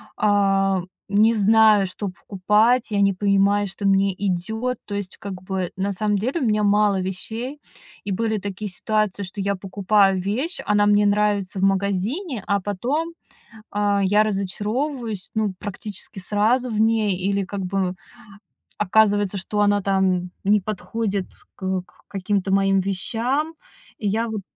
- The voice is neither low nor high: No, high, 205 Hz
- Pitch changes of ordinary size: No, narrow, 1.9 semitones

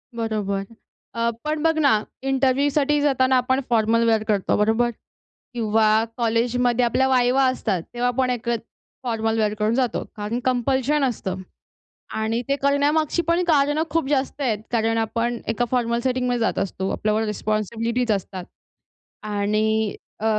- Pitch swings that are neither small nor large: Yes, average, 3.3 semitones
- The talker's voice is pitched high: Yes, high, 235 Hz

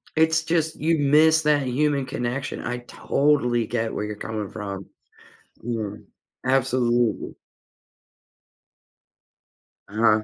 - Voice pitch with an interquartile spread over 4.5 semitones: Yes, average, 5.0 semitones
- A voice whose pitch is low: Yes, low, 125 Hz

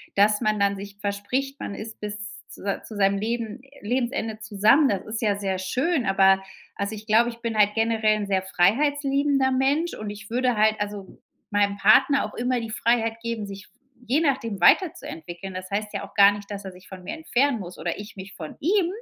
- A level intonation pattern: No, average, 3.7 semitones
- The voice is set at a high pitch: Yes, high, 215 Hz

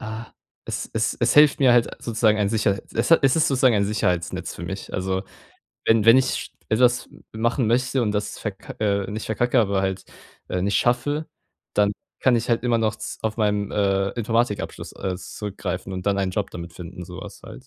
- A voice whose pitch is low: Yes, low, 105 Hz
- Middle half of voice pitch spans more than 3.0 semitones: Yes, average, 3.5 semitones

